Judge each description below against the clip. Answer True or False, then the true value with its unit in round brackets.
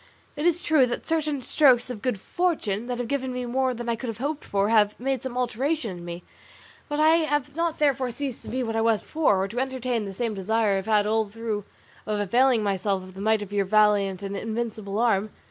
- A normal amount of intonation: True (4.3 semitones)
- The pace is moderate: False (235 wpm)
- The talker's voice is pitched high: True (230 Hz)